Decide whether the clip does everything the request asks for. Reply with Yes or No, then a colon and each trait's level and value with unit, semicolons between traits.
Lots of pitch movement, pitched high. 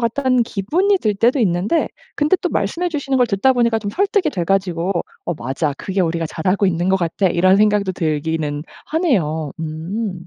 Yes: wide, 6.6 semitones; high, 195 Hz